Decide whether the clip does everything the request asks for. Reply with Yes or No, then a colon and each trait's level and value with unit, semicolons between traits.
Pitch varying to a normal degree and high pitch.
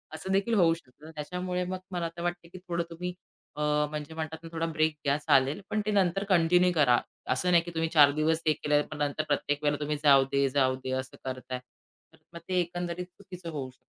No: average, 3.5 semitones; medium, 160 Hz